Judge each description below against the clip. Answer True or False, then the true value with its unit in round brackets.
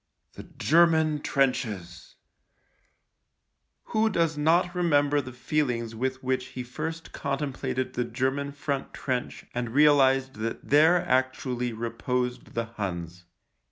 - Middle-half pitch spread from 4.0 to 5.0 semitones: False (3.4 semitones)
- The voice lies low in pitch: True (130 Hz)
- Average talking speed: False (115 wpm)